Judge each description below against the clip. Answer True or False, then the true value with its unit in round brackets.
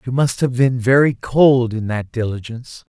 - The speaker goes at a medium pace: True (185 wpm)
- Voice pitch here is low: True (120 Hz)